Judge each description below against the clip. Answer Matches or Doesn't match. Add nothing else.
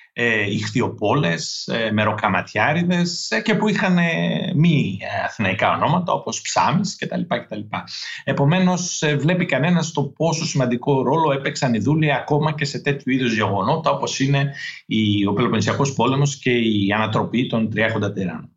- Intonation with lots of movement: Matches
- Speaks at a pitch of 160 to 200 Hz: Doesn't match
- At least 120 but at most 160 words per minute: Matches